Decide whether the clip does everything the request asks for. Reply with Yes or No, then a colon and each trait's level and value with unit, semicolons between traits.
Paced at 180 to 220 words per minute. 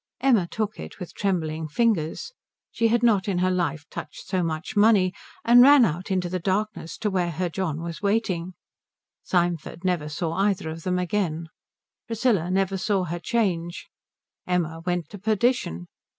No: average, 165 wpm